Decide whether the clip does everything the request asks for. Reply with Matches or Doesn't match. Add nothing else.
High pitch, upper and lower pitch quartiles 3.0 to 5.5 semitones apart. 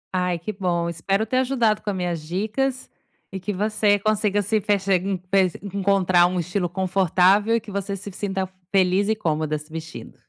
Doesn't match